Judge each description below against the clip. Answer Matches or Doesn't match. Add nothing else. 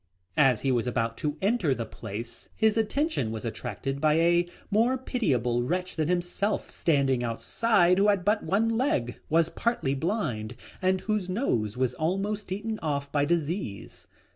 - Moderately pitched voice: Matches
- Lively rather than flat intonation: Matches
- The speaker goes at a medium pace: Matches